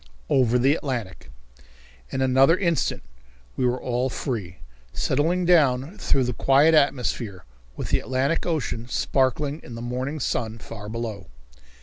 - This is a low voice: Yes, low, 130 Hz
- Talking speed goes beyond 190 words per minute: No, slow, 135 wpm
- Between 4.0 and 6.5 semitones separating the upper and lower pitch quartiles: No, average, 3.6 semitones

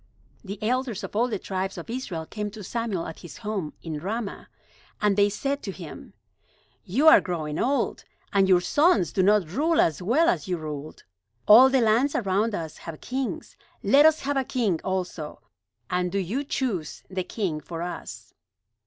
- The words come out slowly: No, average, 180 wpm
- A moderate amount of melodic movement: No, wide, 5.9 semitones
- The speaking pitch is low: No, high, 205 Hz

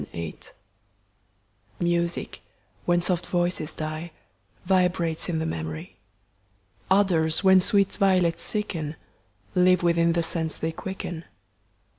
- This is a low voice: No, medium, 170 Hz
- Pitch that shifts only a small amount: Yes, narrow, 2.3 semitones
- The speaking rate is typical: No, slow, 115 wpm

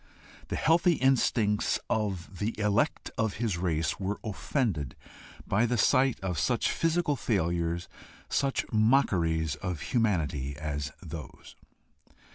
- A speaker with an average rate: No, slow, 115 wpm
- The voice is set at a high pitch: No, low, 100 Hz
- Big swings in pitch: Yes, wide, 6.4 semitones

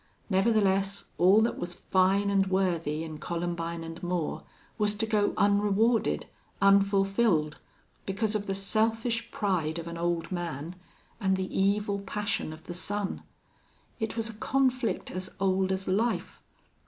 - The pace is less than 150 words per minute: Yes, average, 140 wpm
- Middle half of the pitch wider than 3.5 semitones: No, average, 3.1 semitones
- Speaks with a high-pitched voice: Yes, high, 195 Hz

